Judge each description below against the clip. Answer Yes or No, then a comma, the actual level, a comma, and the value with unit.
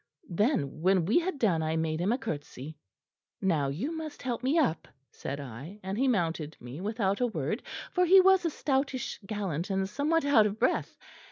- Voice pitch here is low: No, high, 205 Hz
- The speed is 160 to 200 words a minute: Yes, average, 190 wpm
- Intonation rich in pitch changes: Yes, wide, 8.8 semitones